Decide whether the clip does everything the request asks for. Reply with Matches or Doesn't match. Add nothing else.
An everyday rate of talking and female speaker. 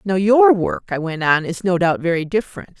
Doesn't match